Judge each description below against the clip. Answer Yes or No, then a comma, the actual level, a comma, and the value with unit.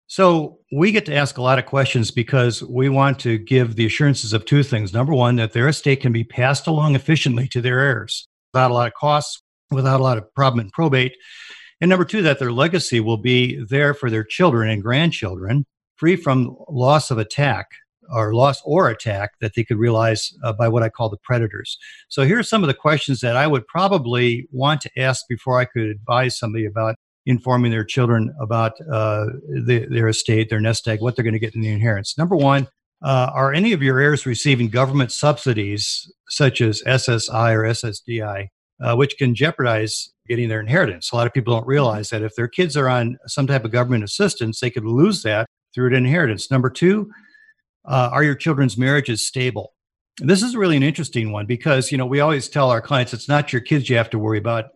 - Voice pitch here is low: Yes, low, 125 Hz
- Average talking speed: No, fast, 215 wpm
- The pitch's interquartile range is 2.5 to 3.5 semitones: No, average, 3.9 semitones